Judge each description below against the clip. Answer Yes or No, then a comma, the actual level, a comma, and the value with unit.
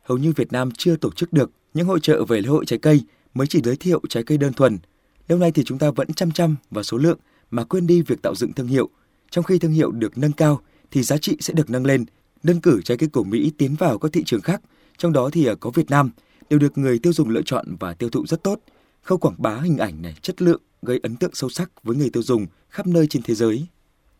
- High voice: No, medium, 150 Hz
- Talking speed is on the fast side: Yes, fast, 270 wpm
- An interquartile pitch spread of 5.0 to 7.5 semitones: Yes, wide, 5.6 semitones